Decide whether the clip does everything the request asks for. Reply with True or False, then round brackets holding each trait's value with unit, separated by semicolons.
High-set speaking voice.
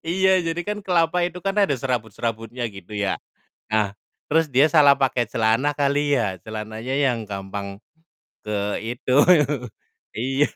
False (125 Hz)